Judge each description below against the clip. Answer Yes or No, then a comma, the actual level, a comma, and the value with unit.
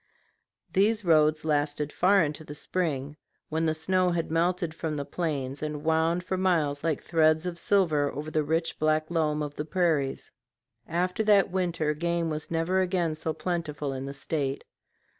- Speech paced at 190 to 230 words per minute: No, average, 170 wpm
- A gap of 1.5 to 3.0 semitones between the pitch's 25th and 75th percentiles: Yes, narrow, 2.6 semitones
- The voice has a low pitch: No, medium, 160 Hz